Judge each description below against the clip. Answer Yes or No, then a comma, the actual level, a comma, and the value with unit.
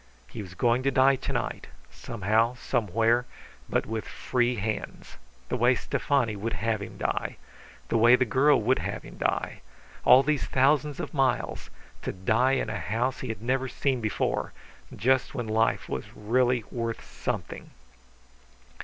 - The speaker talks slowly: No, average, 160 wpm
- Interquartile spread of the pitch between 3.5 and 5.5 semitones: No, average, 2.8 semitones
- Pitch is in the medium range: No, low, 120 Hz